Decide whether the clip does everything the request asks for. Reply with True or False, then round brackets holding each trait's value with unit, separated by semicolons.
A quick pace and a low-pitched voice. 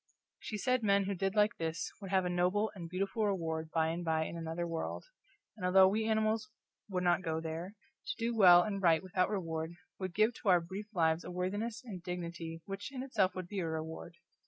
False (215 wpm; 185 Hz)